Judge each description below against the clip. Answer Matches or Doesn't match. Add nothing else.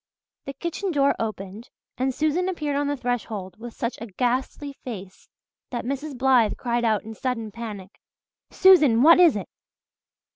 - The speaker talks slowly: Doesn't match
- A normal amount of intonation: Matches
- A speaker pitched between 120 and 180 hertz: Doesn't match